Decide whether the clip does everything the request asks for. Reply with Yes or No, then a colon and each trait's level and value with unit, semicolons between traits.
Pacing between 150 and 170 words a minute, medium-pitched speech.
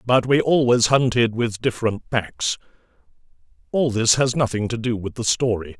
No: average, 165 wpm; low, 115 Hz